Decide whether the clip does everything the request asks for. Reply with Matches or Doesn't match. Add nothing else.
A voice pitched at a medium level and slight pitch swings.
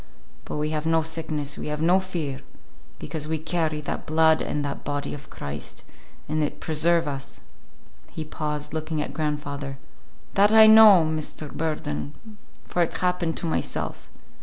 Matches